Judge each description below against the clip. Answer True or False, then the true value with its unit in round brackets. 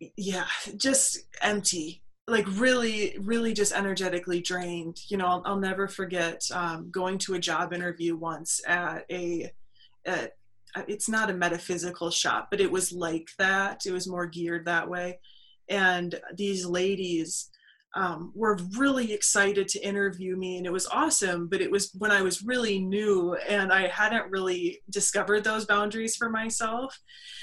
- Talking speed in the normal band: True (160 wpm)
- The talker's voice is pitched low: False (190 Hz)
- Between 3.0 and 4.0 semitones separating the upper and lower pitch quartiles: False (2.6 semitones)